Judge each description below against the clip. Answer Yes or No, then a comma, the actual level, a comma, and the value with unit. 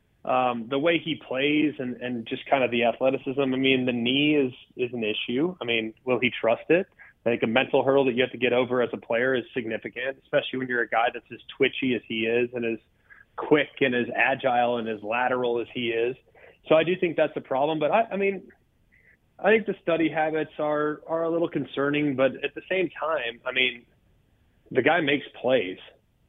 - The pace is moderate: No, fast, 220 wpm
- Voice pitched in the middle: No, low, 130 Hz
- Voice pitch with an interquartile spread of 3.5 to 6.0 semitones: Yes, average, 4.0 semitones